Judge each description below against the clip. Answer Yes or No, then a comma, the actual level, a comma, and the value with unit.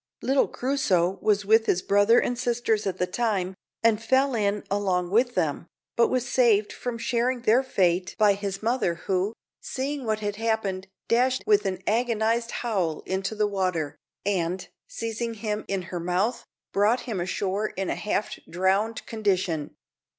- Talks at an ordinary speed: Yes, average, 160 wpm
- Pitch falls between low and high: No, high, 210 Hz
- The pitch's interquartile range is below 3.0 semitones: No, average, 3.8 semitones